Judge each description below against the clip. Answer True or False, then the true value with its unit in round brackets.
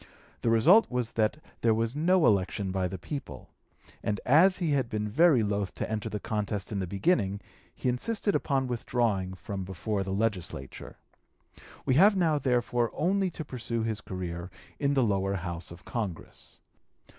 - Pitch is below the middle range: True (110 Hz)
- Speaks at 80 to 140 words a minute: False (170 wpm)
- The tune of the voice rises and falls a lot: True (6.0 semitones)